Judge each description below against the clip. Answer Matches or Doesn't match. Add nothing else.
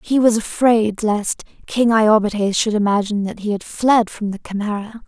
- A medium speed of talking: Matches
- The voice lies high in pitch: Matches